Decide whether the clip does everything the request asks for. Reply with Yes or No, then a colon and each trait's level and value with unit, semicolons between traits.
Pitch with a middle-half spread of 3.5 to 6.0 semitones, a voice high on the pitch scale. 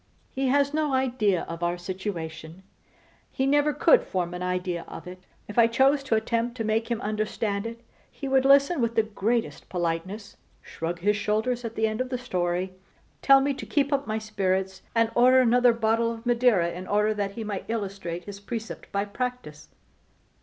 Yes: average, 4.7 semitones; high, 220 Hz